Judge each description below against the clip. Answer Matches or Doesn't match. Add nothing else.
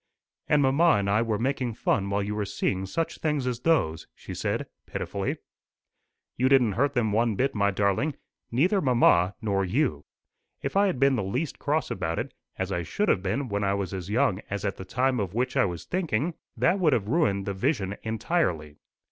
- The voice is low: Matches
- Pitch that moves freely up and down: Matches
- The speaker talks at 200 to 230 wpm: Matches